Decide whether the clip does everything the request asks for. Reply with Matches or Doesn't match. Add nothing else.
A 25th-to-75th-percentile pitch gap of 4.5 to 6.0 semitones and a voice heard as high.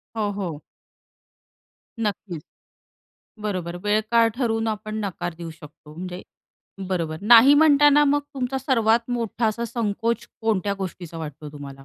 Matches